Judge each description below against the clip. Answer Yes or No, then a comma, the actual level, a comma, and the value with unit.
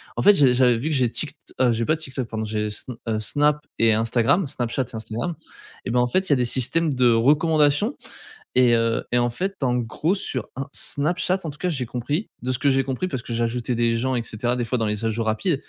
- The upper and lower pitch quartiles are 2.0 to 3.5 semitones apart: No, average, 4.2 semitones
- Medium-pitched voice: No, low, 125 Hz